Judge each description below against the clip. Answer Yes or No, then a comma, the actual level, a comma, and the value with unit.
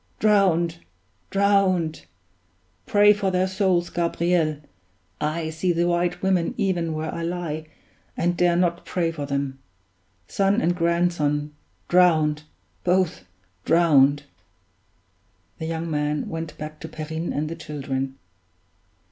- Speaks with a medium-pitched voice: Yes, medium, 170 Hz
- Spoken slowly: Yes, slow, 120 wpm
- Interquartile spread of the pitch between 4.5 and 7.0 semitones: No, narrow, 2.5 semitones